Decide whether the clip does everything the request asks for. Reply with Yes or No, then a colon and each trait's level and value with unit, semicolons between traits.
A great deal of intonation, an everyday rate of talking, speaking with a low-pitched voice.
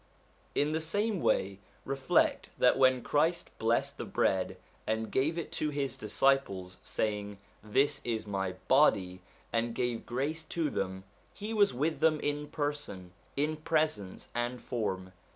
Yes: wide, 6.6 semitones; average, 150 wpm; low, 130 Hz